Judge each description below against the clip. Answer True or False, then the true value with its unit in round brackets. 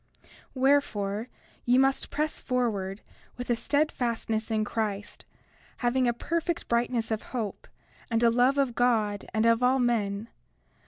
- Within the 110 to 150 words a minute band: True (145 wpm)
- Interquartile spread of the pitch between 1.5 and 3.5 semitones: True (2.7 semitones)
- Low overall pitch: False (235 Hz)